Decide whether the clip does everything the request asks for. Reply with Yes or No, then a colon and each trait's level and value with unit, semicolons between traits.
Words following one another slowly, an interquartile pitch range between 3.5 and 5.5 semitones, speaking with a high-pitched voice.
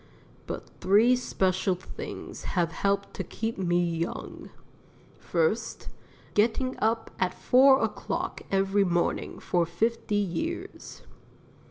Yes: slow, 110 wpm; average, 4.5 semitones; high, 200 Hz